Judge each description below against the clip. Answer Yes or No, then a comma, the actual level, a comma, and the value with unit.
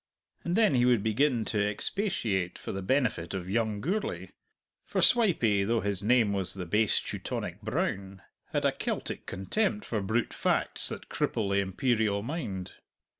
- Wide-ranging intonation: No, average, 4.5 semitones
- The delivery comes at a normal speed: Yes, average, 160 wpm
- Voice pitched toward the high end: No, low, 110 Hz